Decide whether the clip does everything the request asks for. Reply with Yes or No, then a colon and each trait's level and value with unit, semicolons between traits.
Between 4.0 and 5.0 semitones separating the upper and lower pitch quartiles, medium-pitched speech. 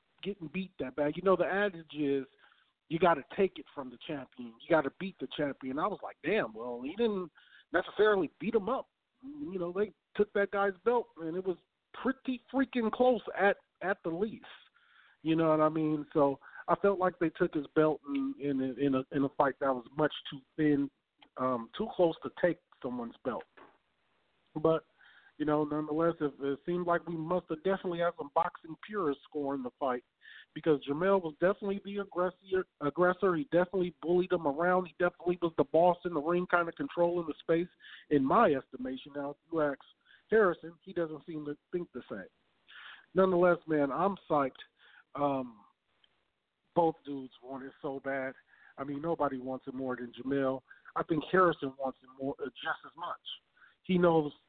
Yes: average, 4.3 semitones; medium, 160 Hz